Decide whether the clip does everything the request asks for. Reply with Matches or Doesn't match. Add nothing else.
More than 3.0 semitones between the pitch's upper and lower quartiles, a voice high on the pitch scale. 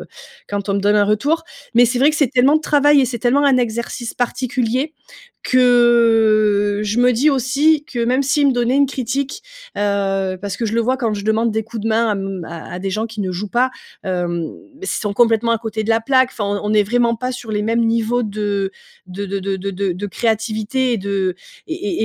Matches